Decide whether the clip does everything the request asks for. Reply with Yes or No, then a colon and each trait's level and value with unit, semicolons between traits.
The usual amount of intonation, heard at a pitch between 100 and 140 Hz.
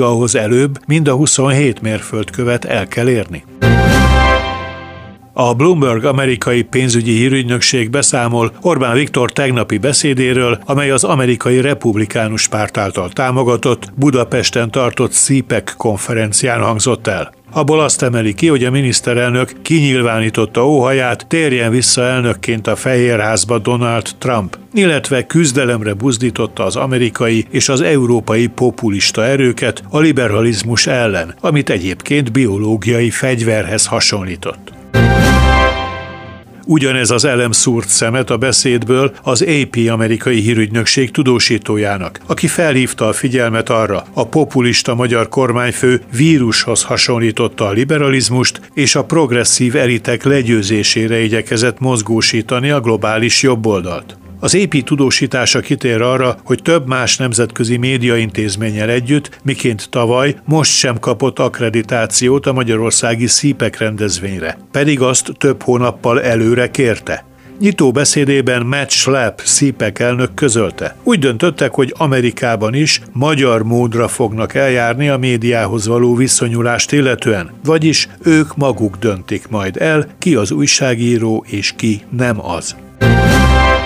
Yes: average, 3.1 semitones; low, 120 Hz